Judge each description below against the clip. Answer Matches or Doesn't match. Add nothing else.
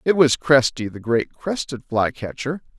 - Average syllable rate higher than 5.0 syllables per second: Doesn't match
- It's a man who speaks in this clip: Matches